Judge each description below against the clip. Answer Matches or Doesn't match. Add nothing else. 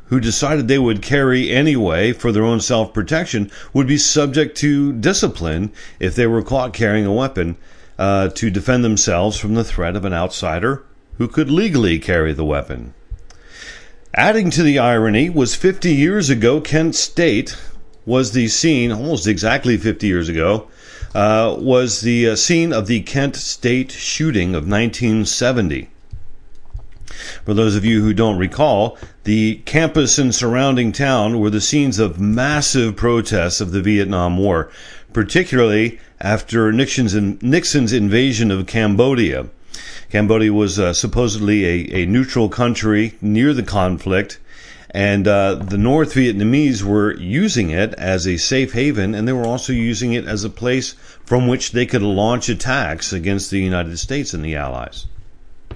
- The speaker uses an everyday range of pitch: Matches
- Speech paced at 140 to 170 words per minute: Matches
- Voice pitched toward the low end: Matches